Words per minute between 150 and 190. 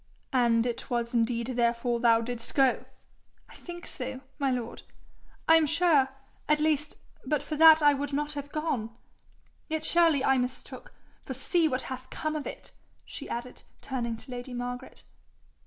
Yes: average, 165 wpm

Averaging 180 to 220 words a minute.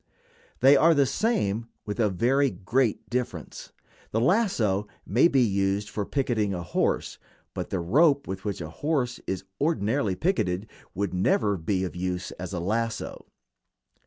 No: average, 155 wpm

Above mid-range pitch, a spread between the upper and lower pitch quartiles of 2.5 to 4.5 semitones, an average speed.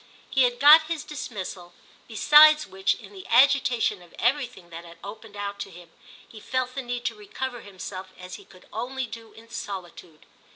No: high, 225 Hz; average, 5.3 semitones; average, 180 wpm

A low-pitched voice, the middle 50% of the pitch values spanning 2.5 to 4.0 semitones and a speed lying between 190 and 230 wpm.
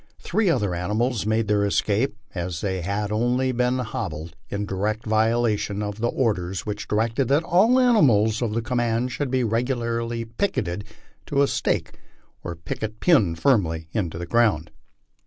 No: low, 110 Hz; average, 3.6 semitones; average, 165 wpm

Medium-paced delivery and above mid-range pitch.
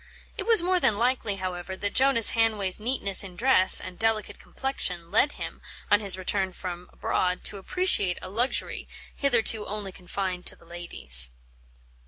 Yes: average, 160 wpm; high, 200 Hz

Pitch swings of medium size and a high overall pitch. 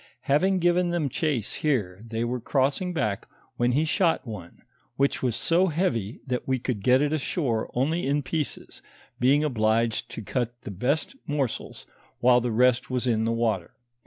No: average, 4.6 semitones; low, 125 Hz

